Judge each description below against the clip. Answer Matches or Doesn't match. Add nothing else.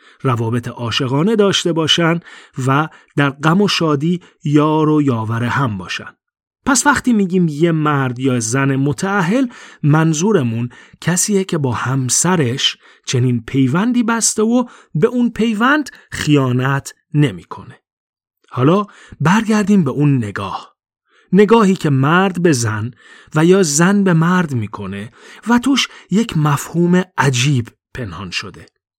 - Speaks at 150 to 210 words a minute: Doesn't match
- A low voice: Doesn't match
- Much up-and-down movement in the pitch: Matches